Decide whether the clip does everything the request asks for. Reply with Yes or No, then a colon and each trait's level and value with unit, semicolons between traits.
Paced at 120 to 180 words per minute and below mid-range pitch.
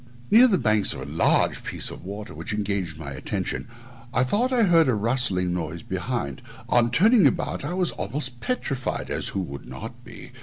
No: average, 195 wpm; low, 115 Hz